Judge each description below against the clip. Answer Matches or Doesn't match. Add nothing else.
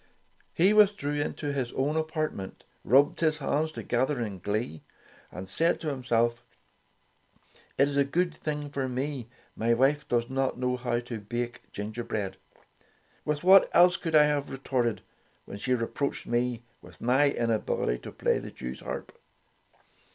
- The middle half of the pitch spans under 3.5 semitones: Doesn't match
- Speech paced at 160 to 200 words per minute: Doesn't match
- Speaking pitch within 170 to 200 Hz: Doesn't match